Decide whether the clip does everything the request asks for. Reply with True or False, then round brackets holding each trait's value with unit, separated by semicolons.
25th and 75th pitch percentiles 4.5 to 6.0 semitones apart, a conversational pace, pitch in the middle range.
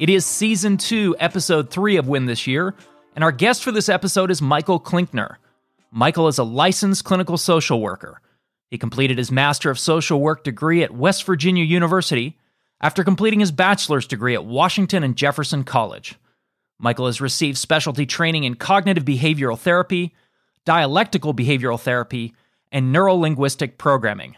True (5.5 semitones; 155 wpm; 160 Hz)